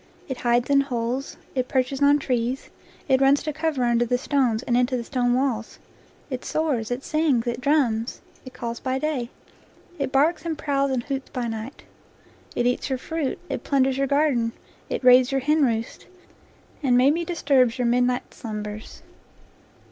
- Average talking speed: Yes, average, 170 wpm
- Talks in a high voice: Yes, very high, 260 Hz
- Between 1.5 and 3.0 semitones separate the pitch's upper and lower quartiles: Yes, average, 2.7 semitones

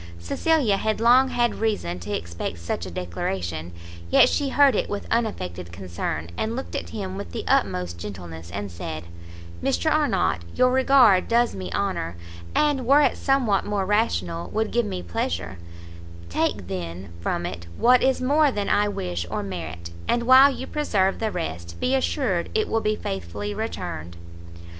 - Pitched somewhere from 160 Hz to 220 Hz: No, low, 100 Hz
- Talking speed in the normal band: Yes, average, 165 wpm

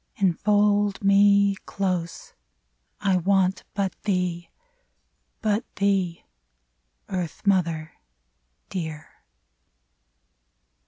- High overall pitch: Yes, high, 195 Hz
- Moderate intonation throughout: No, narrow, 2.3 semitones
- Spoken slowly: Yes, slow, 75 wpm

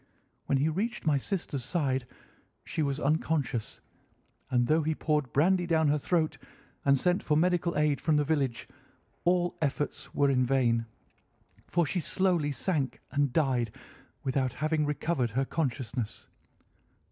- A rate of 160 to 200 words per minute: No, average, 145 wpm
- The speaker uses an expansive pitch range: No, average, 3.4 semitones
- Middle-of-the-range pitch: Yes, medium, 150 Hz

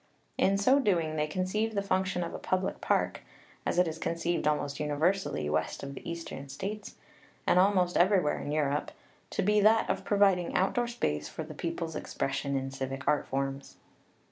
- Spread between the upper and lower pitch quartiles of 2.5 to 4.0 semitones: No, average, 5.2 semitones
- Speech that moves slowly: No, average, 175 wpm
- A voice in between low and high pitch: Yes, medium, 170 Hz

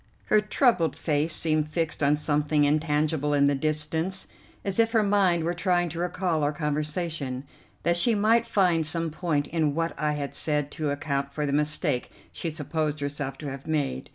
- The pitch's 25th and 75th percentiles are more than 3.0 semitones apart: No, average, 2.7 semitones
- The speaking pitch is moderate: Yes, medium, 155 Hz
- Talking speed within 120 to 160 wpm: No, average, 180 wpm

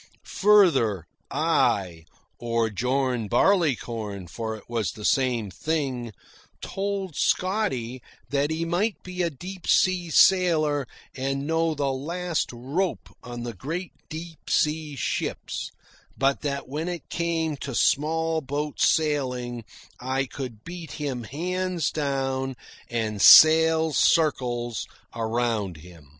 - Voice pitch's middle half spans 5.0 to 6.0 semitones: Yes, wide, 5.4 semitones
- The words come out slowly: Yes, slow, 120 wpm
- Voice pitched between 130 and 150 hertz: Yes, medium, 140 Hz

